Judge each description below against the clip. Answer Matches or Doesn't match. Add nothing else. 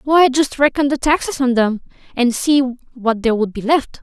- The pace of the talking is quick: Matches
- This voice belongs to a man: Doesn't match